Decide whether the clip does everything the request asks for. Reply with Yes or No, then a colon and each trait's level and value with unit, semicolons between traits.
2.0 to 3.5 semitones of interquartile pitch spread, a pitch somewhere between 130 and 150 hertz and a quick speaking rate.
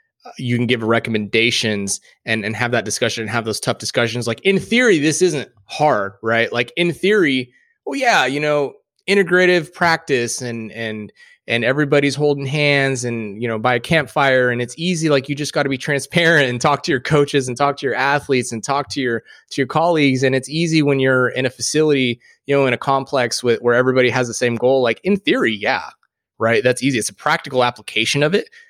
No: average, 3.9 semitones; low, 135 Hz; fast, 215 wpm